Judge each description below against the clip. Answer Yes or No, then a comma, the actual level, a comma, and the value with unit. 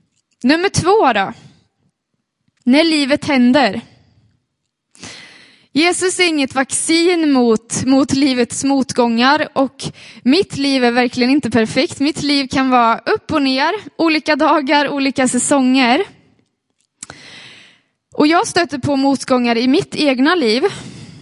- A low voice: No, very high, 275 Hz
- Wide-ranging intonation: No, average, 3.5 semitones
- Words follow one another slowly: Yes, slow, 115 wpm